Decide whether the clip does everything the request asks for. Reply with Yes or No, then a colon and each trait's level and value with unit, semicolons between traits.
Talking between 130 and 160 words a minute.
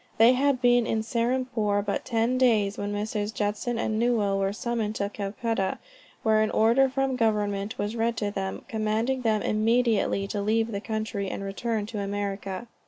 No: average, 170 wpm